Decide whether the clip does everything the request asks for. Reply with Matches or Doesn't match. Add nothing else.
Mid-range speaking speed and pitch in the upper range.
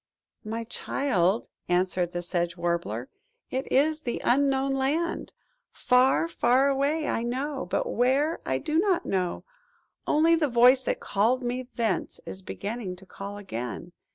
Matches